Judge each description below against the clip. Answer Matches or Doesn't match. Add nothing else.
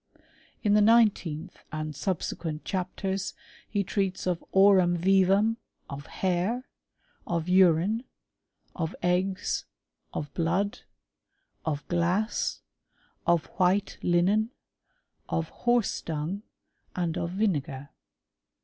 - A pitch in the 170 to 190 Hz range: Matches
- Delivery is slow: Matches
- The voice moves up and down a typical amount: Matches